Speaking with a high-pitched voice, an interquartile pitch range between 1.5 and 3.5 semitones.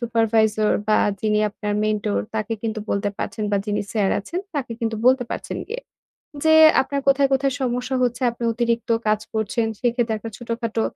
Yes: high, 230 Hz; narrow, 2.6 semitones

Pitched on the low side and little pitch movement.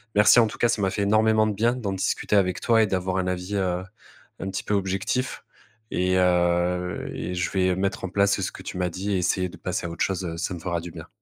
Yes: very low, 95 Hz; narrow, 2.1 semitones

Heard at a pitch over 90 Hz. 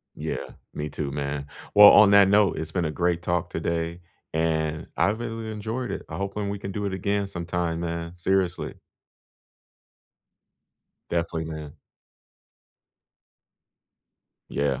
No: very low, 85 Hz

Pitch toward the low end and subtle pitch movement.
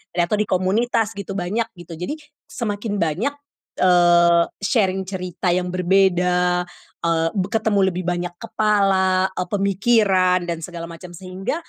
No: medium, 185 Hz; narrow, 2.3 semitones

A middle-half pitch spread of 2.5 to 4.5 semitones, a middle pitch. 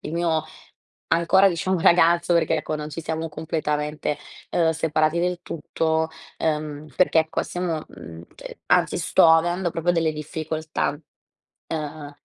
No: narrow, 1.7 semitones; medium, 160 Hz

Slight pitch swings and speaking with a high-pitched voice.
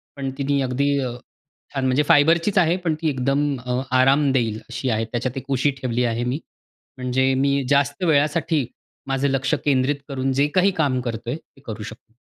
No: narrow, 2.3 semitones; low, 135 Hz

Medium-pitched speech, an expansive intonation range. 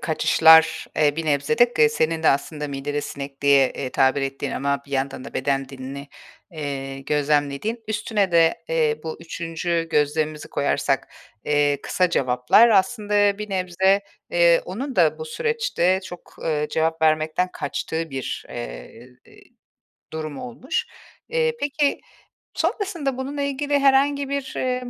Yes: medium, 160 Hz; wide, 7.7 semitones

